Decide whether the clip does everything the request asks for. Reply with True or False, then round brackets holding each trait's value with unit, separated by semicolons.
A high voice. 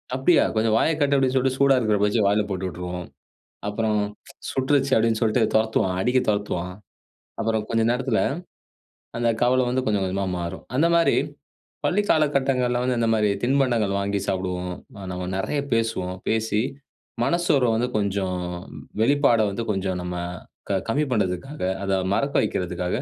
False (110 Hz)